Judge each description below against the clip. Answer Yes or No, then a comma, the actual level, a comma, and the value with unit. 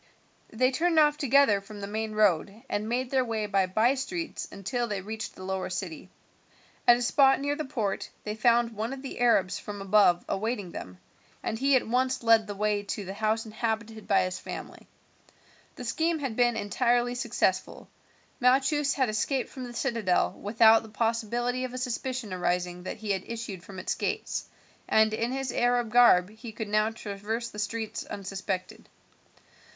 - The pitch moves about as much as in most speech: Yes, average, 3.3 semitones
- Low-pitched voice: No, high, 225 Hz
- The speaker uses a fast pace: No, average, 175 wpm